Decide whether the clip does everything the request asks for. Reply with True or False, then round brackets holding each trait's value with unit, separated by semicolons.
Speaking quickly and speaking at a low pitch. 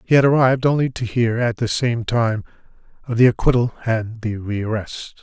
False (185 wpm; 120 Hz)